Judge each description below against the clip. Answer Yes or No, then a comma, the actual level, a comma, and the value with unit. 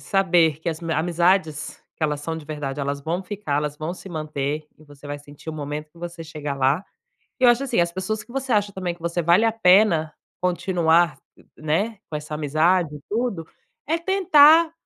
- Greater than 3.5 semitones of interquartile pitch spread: Yes, average, 4.3 semitones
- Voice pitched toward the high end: No, medium, 170 Hz